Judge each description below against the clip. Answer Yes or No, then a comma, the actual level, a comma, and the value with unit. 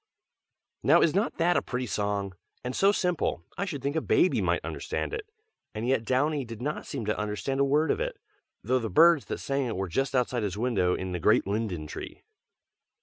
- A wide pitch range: Yes, wide, 6.5 semitones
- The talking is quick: Yes, fast, 210 wpm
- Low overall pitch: Yes, low, 125 Hz